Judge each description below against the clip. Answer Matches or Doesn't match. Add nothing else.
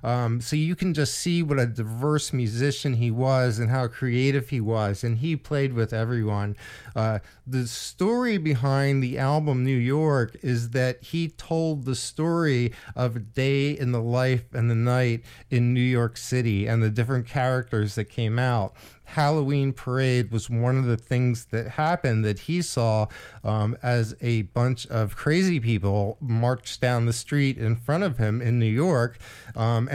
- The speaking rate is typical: Matches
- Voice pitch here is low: Matches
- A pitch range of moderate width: Matches